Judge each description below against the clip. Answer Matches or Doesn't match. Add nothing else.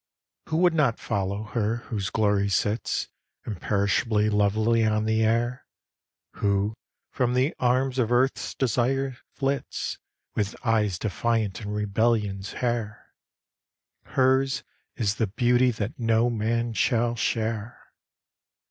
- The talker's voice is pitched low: Matches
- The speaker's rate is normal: Doesn't match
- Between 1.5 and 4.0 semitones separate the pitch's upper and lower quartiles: Matches